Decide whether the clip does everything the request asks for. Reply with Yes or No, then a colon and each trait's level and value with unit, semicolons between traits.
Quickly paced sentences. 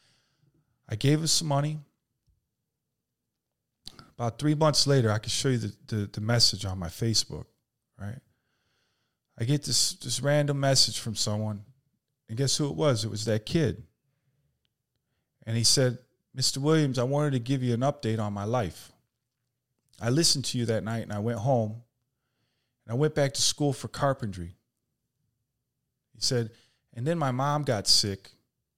No: average, 165 wpm